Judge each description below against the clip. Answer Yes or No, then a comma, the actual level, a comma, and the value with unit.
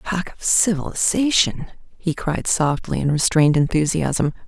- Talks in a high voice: No, medium, 165 Hz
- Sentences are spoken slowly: Yes, slow, 120 wpm